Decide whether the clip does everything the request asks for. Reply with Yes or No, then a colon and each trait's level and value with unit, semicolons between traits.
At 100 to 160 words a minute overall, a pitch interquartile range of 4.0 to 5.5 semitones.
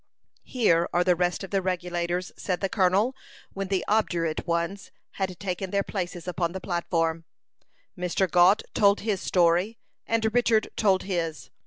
No: average, 155 wpm; narrow, 2.4 semitones